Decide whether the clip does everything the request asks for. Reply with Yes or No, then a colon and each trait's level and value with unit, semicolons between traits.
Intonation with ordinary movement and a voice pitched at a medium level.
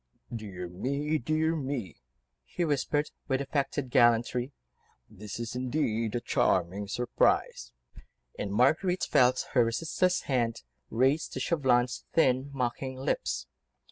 No: average, 3.8 semitones; low, 125 Hz